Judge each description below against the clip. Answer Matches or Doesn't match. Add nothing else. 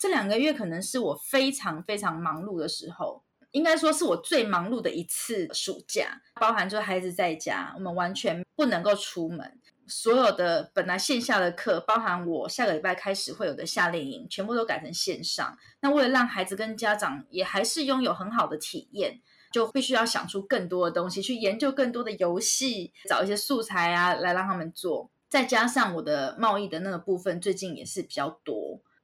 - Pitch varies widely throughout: Matches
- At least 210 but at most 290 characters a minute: Doesn't match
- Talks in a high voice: Matches